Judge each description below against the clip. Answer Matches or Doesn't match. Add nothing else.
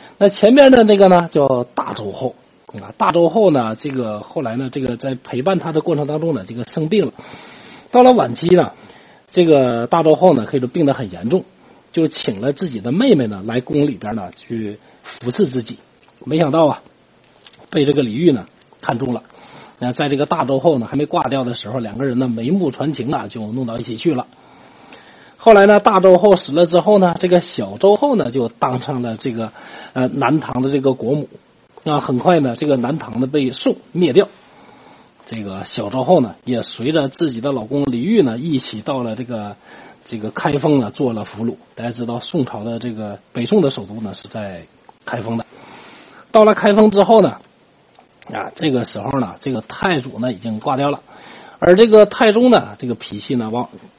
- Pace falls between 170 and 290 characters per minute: Matches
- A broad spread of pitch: Matches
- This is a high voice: Doesn't match